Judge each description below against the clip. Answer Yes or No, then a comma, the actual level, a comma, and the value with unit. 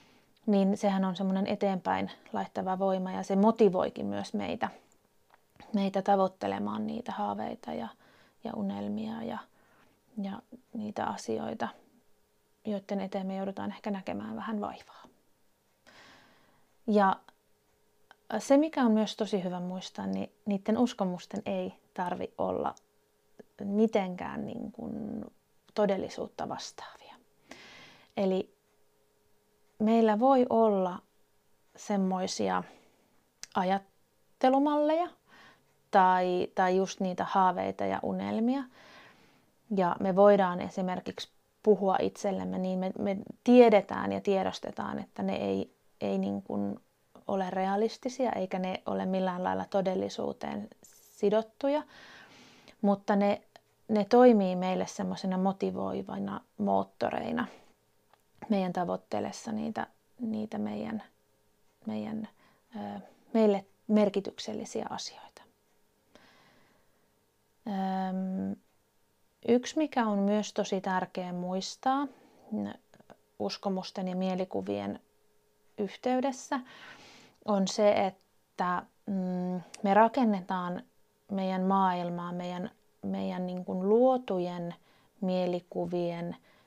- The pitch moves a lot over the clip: No, average, 3.2 semitones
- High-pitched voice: Yes, high, 195 Hz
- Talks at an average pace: No, slow, 90 wpm